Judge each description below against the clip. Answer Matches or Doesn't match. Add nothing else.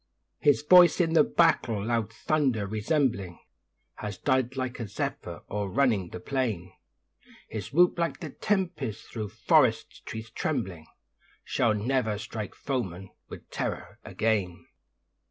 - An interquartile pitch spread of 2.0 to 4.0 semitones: Doesn't match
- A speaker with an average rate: Doesn't match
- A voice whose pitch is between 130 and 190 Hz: Doesn't match